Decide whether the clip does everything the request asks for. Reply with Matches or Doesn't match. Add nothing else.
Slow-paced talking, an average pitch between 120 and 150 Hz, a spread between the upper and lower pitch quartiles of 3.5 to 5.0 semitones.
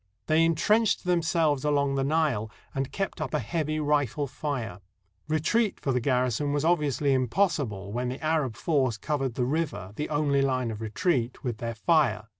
Doesn't match